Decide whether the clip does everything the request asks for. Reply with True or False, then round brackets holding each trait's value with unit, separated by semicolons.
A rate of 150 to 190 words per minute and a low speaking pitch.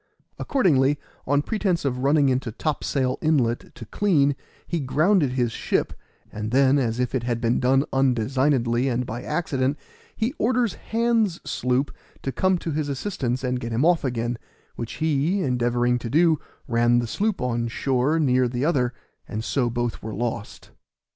True (165 wpm; 130 Hz)